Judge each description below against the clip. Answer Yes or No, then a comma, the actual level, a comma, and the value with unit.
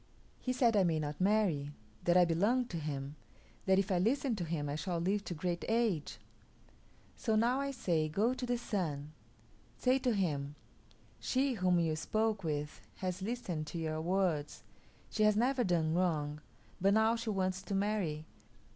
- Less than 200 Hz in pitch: Yes, medium, 185 Hz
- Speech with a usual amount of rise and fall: No, wide, 5.8 semitones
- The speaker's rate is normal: Yes, average, 175 wpm